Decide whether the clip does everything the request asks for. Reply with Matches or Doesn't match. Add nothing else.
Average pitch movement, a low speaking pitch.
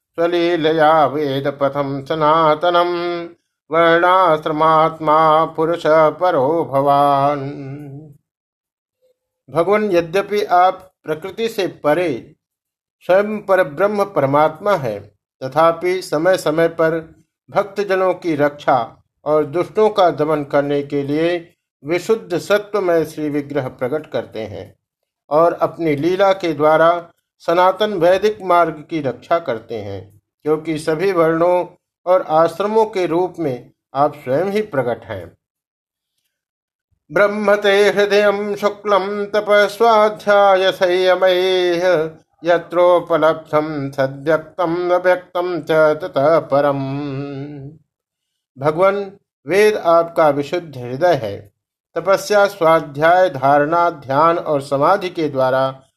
Doesn't match